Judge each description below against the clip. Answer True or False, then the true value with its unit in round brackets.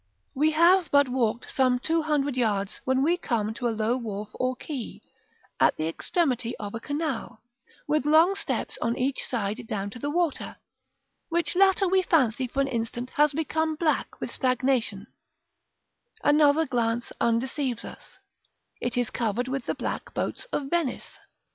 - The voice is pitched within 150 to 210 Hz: False (260 Hz)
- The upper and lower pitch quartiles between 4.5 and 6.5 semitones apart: True (4.8 semitones)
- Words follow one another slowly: False (165 wpm)